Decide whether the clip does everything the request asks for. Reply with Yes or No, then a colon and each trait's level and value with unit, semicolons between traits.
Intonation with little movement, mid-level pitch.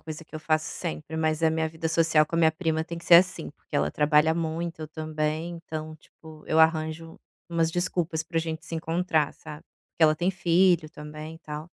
Yes: narrow, 1.2 semitones; medium, 160 Hz